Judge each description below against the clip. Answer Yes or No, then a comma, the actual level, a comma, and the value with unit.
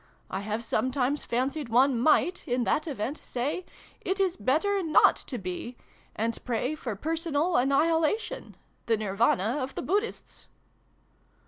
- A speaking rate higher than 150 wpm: No, average, 140 wpm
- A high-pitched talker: Yes, very high, 265 Hz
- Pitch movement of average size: No, wide, 5.7 semitones